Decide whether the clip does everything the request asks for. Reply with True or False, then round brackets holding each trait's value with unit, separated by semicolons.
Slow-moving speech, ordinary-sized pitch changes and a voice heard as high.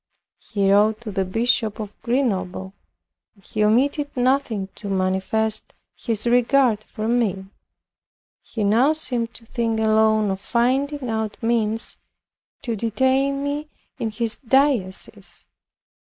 True (125 wpm; 3.2 semitones; 225 Hz)